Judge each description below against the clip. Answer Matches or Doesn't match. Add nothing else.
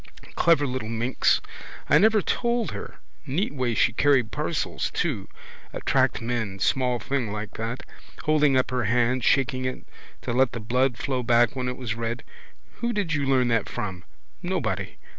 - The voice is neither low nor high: Doesn't match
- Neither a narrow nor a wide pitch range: Matches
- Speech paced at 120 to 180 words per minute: Matches